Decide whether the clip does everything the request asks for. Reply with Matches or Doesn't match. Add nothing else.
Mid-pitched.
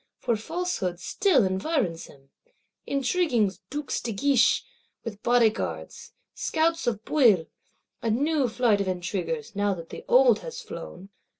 Doesn't match